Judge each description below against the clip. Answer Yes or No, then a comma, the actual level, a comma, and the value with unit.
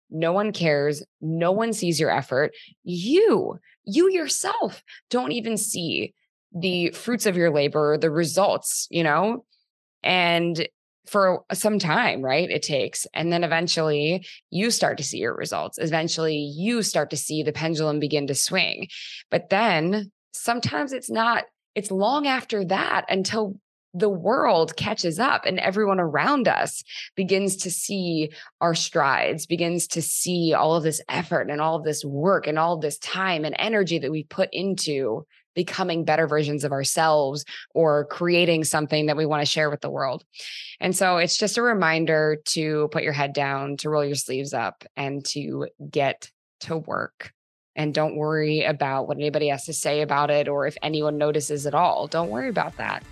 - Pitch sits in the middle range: Yes, medium, 165 Hz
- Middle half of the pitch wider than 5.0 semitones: No, average, 4.2 semitones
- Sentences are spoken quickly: No, average, 175 wpm